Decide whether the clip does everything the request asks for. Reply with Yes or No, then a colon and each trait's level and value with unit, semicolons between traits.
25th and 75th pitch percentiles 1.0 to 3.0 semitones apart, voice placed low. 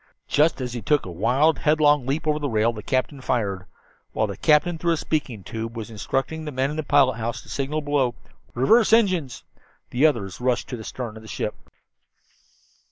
No: average, 4.8 semitones; low, 130 Hz